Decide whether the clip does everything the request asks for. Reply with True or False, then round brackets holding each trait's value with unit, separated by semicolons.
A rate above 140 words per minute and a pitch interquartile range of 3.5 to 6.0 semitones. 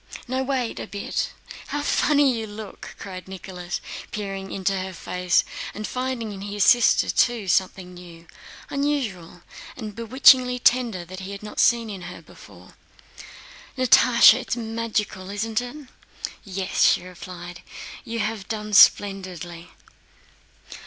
False (135 wpm; 4.2 semitones)